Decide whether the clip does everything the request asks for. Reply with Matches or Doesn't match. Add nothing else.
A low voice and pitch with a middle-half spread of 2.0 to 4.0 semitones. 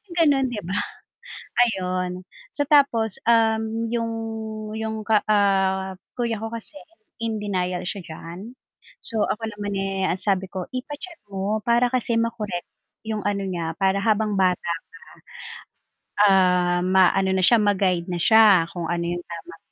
Doesn't match